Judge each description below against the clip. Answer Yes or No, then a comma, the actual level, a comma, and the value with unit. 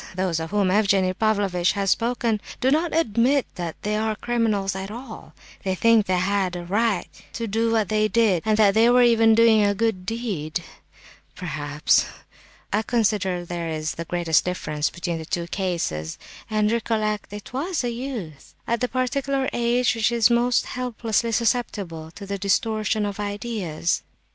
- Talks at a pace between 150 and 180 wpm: Yes, average, 165 wpm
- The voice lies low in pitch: No, high, 210 Hz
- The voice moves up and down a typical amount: Yes, average, 4.1 semitones